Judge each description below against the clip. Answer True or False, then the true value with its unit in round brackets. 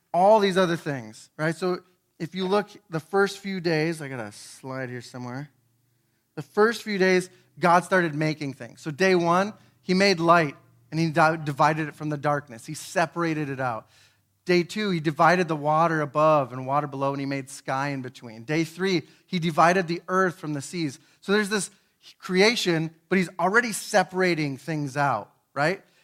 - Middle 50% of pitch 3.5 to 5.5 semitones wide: True (4.6 semitones)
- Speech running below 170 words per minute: False (185 wpm)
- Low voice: False (160 Hz)